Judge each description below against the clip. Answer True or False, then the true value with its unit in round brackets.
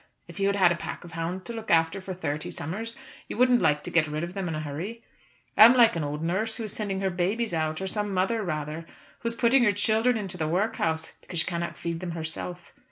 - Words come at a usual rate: False (250 wpm)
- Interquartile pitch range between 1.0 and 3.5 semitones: False (4.9 semitones)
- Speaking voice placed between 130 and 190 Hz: True (185 Hz)